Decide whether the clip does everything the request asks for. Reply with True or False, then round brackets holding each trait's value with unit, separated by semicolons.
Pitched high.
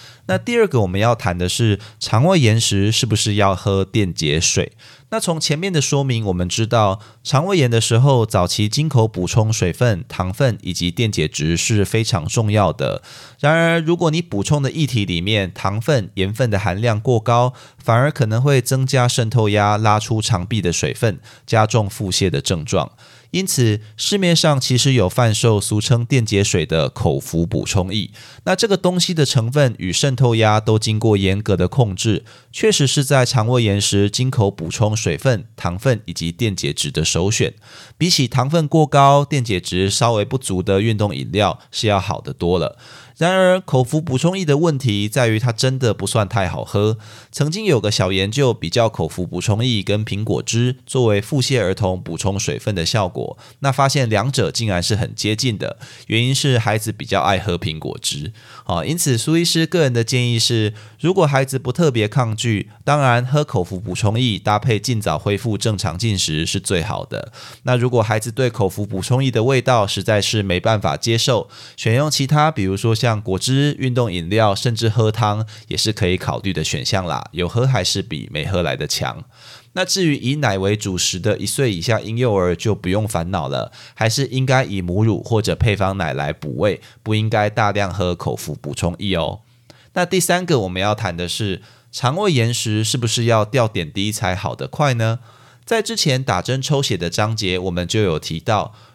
False (115 Hz)